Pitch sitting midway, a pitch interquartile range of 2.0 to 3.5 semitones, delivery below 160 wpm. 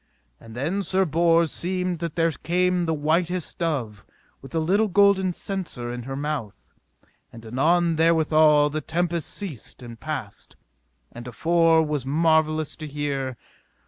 No: medium, 160 Hz; average, 4.0 semitones; average, 145 wpm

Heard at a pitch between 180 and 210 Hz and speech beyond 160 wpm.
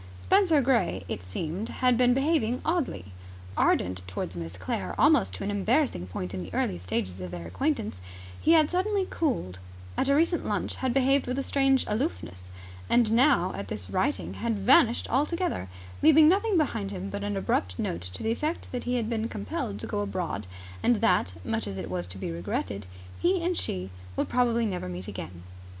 No: high, 220 Hz; average, 190 wpm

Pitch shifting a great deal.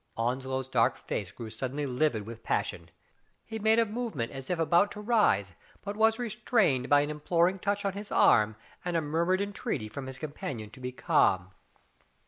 Yes: wide, 8.3 semitones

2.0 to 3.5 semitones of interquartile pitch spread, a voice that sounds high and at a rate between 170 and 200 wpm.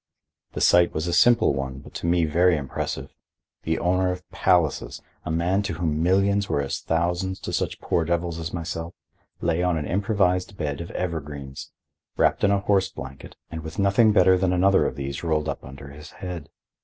No: average, 3.1 semitones; very low, 85 Hz; average, 190 wpm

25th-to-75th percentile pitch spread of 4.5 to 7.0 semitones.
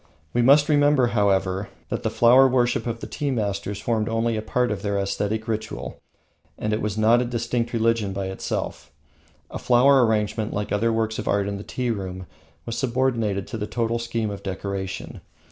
No: average, 2.9 semitones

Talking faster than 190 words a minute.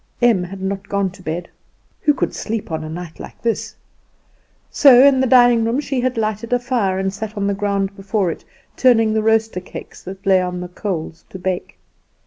Yes: fast, 205 wpm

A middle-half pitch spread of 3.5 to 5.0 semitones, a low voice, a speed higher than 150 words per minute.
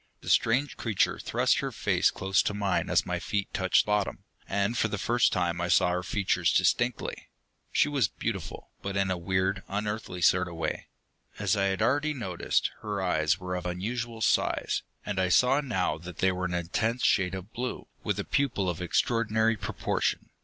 Yes: average, 3.8 semitones; low, 100 Hz; average, 190 wpm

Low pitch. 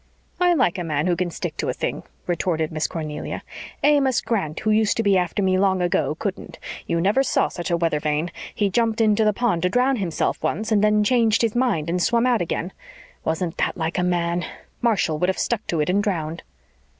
No: medium, 185 Hz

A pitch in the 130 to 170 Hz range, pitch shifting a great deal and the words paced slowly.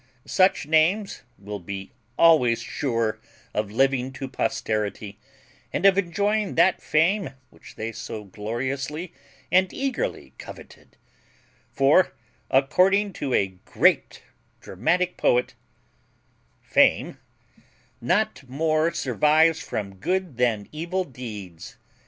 Yes: low, 135 Hz; wide, 8.4 semitones; slow, 105 wpm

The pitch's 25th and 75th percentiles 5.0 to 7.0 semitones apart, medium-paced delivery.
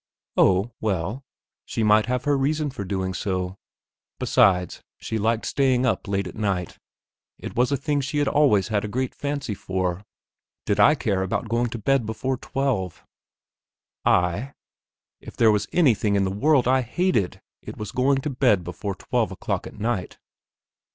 Yes: wide, 5.5 semitones; average, 170 wpm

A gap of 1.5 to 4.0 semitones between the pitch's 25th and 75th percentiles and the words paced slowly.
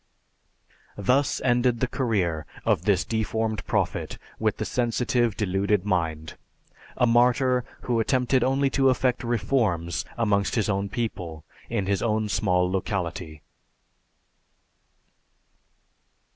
No: average, 4.6 semitones; slow, 110 wpm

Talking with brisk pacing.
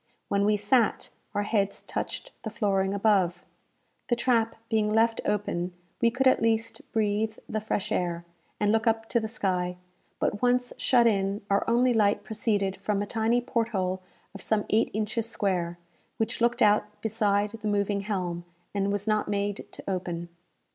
No: average, 170 wpm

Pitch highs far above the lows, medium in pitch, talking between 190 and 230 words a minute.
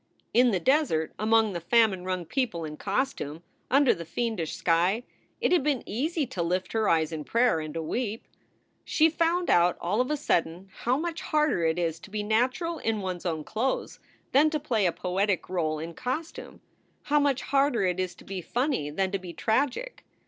No: wide, 7.5 semitones; high, 215 Hz; average, 200 wpm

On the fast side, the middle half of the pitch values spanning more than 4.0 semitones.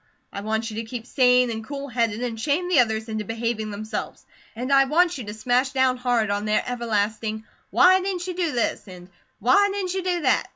Yes: fast, 215 wpm; average, 4.5 semitones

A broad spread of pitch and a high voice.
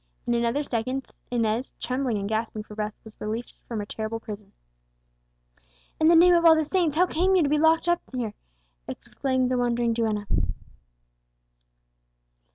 Yes: wide, 5.8 semitones; high, 245 Hz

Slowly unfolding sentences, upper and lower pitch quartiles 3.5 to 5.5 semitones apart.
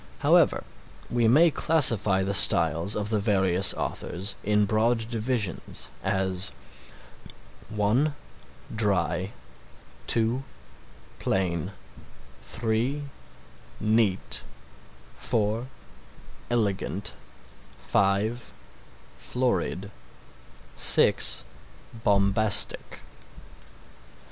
No: slow, 65 wpm; average, 3.1 semitones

